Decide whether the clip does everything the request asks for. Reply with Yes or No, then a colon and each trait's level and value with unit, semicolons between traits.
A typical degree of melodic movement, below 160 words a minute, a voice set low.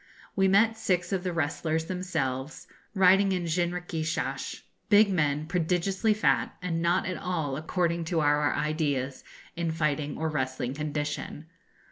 No: average, 3.5 semitones; slow, 135 wpm; medium, 165 Hz